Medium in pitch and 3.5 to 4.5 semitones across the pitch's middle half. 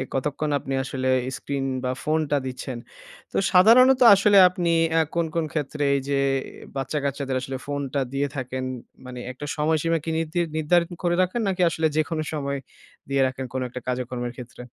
Yes: medium, 145 Hz; average, 3.9 semitones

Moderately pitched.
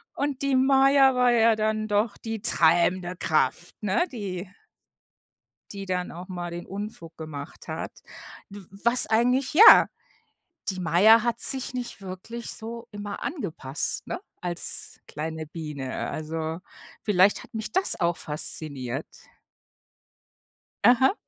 No: high, 200 Hz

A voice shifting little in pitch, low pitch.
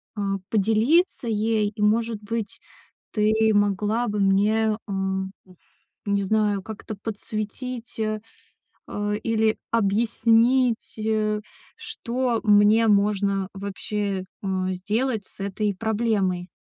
No: narrow, 2.0 semitones; high, 210 Hz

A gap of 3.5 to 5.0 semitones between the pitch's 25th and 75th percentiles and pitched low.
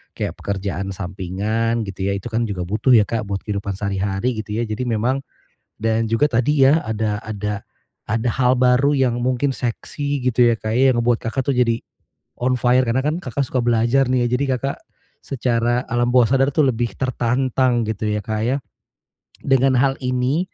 No: average, 3.1 semitones; low, 120 Hz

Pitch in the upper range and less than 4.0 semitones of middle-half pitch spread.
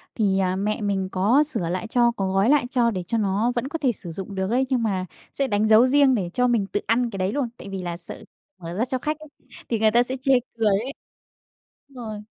No: high, 220 Hz; average, 4.4 semitones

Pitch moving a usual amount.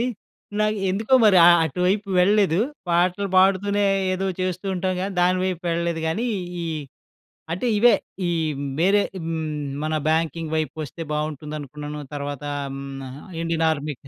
Yes: average, 3.8 semitones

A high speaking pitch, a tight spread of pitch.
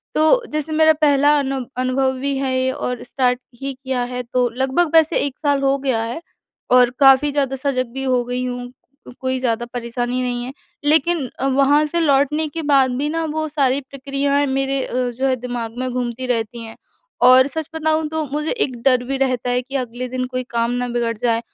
Yes: very high, 260 Hz; narrow, 2.3 semitones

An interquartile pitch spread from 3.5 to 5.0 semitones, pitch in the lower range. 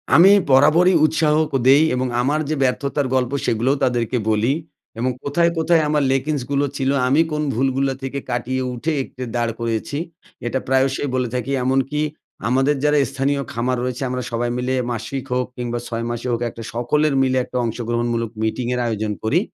No: average, 2.8 semitones; low, 130 Hz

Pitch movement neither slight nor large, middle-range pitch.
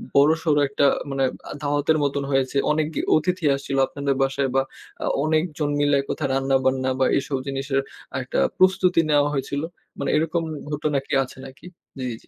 No: narrow, 2.2 semitones; medium, 145 Hz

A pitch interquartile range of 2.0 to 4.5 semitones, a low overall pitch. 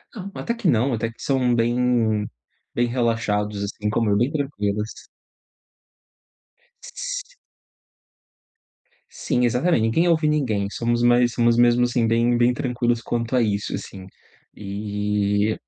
Yes: average, 2.9 semitones; low, 120 Hz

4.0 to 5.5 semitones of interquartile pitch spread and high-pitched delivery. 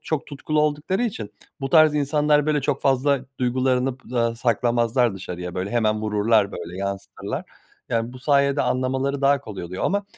No: average, 4.6 semitones; low, 130 Hz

